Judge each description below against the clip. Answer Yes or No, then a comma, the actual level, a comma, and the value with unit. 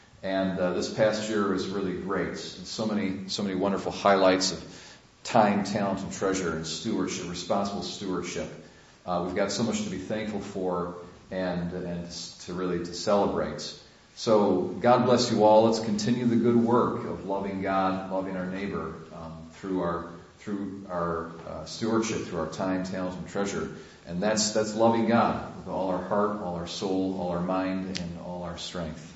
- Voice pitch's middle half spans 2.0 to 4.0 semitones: Yes, average, 3.3 semitones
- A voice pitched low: Yes, very low, 95 Hz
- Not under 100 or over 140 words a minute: No, average, 180 wpm